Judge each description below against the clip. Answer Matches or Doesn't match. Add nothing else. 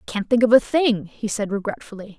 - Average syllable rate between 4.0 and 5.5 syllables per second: Doesn't match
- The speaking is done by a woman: Matches